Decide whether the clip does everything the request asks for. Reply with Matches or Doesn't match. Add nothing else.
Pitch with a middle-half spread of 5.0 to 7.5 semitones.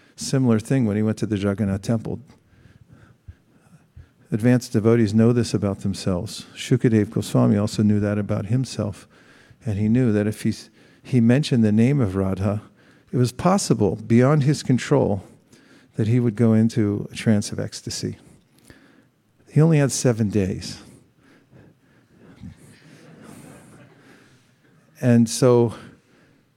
Doesn't match